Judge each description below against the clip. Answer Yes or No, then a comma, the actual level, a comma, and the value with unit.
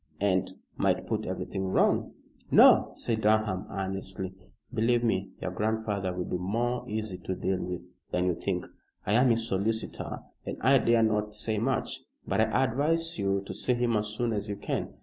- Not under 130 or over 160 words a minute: No, average, 180 wpm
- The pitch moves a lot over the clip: No, average, 3.2 semitones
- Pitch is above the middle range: No, low, 105 Hz